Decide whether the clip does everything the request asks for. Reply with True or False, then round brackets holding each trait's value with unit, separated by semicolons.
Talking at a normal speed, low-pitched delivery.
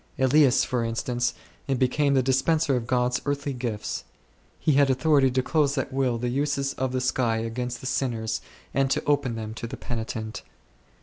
True (175 wpm; 130 Hz)